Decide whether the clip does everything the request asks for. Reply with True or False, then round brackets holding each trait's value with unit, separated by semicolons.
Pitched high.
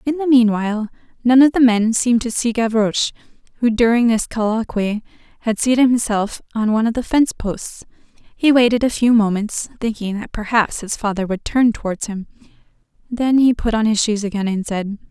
True (225 Hz)